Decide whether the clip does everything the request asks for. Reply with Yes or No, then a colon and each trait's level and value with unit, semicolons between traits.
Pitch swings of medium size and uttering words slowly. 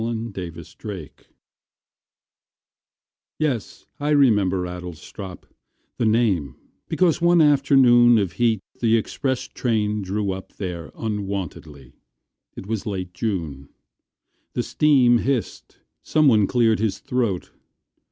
Yes: average, 4.7 semitones; slow, 105 wpm